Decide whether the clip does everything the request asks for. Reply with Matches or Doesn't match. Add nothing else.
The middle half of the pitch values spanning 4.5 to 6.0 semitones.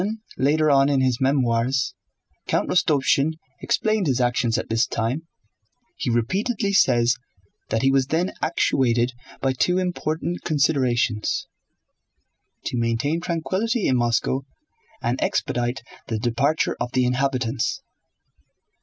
Matches